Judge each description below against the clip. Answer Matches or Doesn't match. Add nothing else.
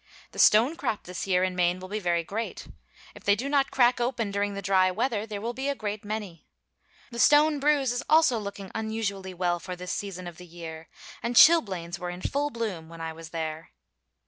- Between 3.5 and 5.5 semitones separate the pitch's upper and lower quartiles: Matches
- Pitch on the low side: Doesn't match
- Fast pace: Matches